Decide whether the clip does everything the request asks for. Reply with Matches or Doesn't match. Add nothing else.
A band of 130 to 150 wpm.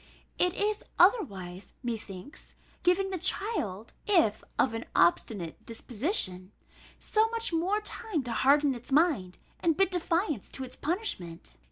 Matches